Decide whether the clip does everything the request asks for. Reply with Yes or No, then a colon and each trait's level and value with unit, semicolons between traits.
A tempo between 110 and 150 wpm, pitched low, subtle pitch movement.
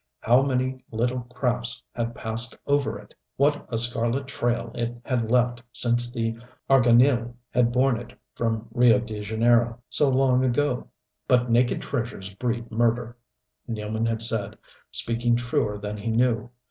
Yes: average, 145 wpm; low, 120 Hz; narrow, 1.6 semitones